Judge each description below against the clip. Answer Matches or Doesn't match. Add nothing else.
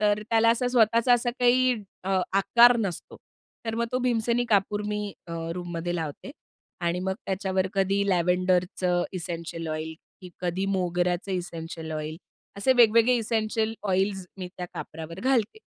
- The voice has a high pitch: Matches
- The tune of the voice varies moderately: Matches